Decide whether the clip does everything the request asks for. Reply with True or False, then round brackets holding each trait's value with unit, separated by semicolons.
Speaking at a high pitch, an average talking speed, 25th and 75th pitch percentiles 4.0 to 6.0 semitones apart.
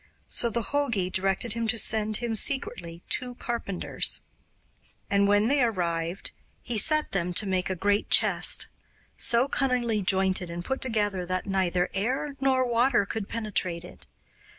True (210 Hz; 150 wpm; 4.4 semitones)